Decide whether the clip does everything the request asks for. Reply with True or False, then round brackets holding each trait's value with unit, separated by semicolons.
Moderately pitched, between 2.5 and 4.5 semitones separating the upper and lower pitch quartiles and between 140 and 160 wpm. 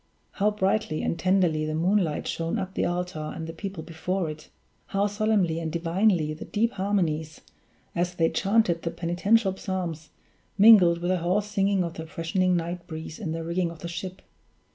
False (175 Hz; 3.0 semitones; 180 wpm)